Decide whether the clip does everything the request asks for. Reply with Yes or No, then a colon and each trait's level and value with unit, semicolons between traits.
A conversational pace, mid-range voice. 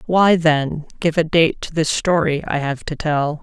No: fast, 210 wpm; medium, 155 Hz